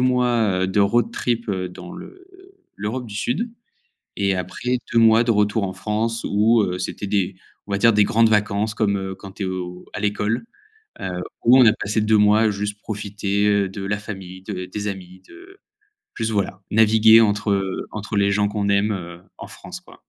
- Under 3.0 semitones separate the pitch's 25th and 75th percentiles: Yes, narrow, 2.4 semitones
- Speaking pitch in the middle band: No, low, 105 Hz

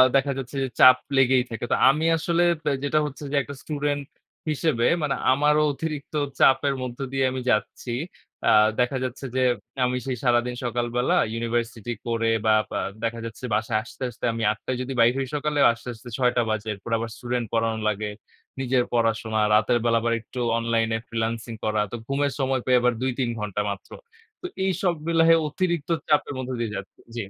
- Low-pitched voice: Yes, low, 125 Hz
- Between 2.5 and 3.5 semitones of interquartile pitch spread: Yes, average, 3.1 semitones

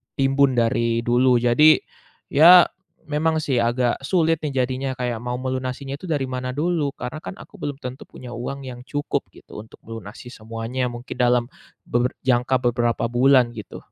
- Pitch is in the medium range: No, low, 130 Hz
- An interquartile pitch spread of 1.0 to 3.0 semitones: Yes, narrow, 2.5 semitones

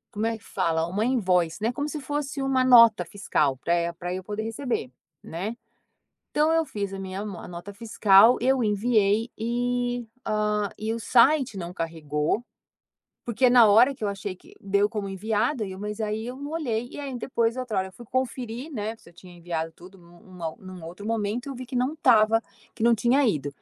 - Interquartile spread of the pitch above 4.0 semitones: Yes, average, 4.5 semitones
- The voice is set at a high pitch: Yes, high, 215 Hz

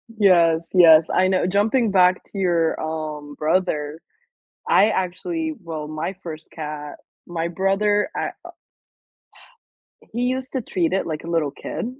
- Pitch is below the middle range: No, medium, 175 Hz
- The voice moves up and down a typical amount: Yes, average, 3.9 semitones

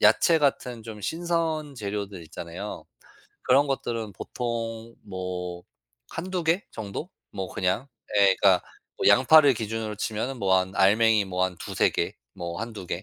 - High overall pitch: No, low, 110 Hz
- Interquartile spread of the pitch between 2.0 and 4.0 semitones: No, wide, 5.4 semitones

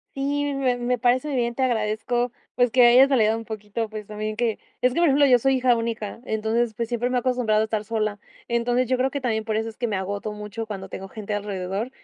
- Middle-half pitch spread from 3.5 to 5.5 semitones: No, average, 2.7 semitones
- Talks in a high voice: Yes, high, 230 Hz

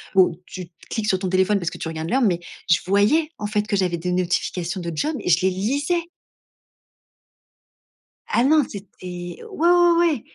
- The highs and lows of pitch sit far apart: Yes, wide, 7.2 semitones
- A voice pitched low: No, high, 195 Hz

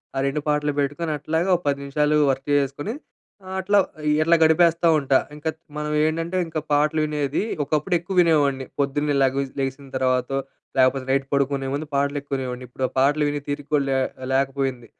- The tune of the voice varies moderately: No, narrow, 2.3 semitones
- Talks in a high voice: No, medium, 145 Hz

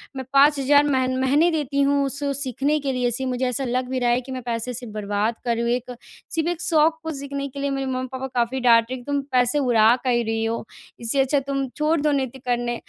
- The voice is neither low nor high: No, very high, 260 Hz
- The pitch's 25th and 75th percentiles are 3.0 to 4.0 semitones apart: No, narrow, 2.5 semitones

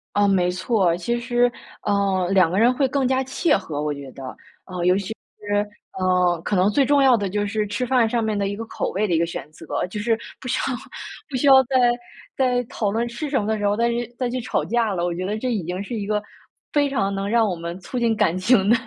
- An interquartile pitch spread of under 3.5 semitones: No, average, 4.5 semitones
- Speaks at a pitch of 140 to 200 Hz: No, high, 210 Hz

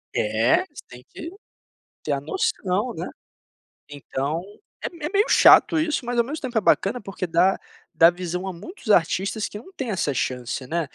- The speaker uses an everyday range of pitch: No, wide, 8.2 semitones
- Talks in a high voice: Yes, high, 195 Hz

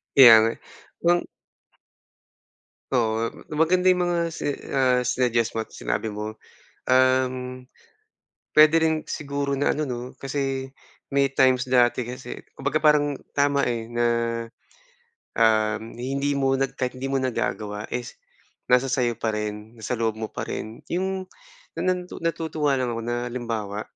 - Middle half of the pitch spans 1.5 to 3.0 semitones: No, average, 3.4 semitones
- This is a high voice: No, low, 130 Hz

